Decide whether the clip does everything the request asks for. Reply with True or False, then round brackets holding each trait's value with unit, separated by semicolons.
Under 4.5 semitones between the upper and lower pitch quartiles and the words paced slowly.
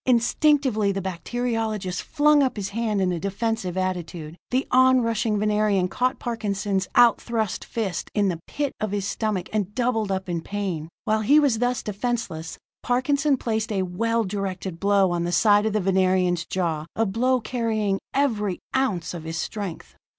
False (3.9 semitones; 165 wpm)